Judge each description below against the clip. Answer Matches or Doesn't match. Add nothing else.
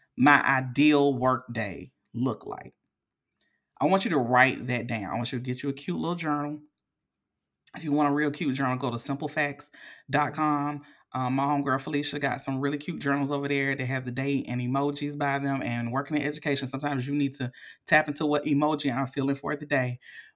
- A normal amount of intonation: Doesn't match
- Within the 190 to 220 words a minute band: Matches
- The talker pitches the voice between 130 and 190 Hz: Matches